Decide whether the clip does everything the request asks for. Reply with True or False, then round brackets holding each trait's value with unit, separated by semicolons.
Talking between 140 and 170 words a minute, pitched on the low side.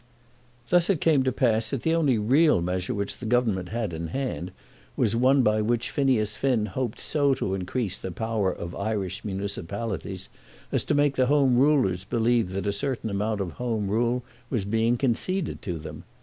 False (185 wpm; 115 Hz)